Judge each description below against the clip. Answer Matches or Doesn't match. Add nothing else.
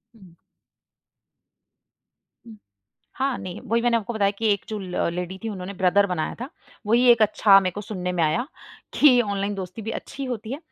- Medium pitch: Doesn't match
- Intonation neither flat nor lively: Matches